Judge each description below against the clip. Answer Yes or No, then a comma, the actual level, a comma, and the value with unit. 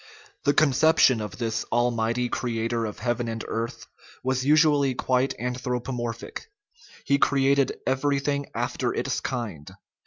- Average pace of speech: No, slow, 130 wpm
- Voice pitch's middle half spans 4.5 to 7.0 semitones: No, average, 2.9 semitones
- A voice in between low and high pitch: No, low, 125 Hz